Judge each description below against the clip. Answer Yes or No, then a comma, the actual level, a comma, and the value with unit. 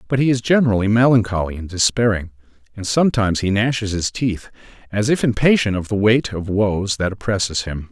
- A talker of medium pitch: No, low, 105 Hz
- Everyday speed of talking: Yes, average, 180 wpm